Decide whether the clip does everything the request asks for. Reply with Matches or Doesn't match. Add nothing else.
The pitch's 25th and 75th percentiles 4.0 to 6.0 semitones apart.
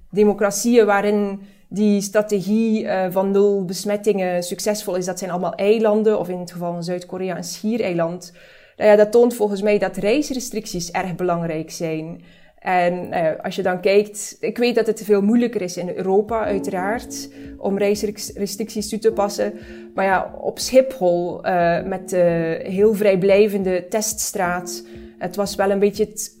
Doesn't match